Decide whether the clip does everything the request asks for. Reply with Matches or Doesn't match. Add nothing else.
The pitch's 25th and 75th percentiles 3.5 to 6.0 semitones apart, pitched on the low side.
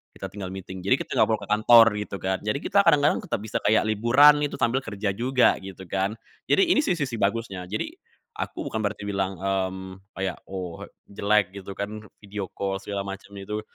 Doesn't match